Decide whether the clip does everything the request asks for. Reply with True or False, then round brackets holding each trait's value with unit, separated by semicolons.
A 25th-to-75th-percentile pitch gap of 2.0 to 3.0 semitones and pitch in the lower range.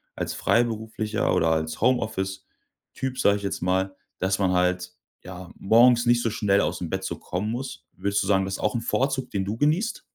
False (4.0 semitones; 100 Hz)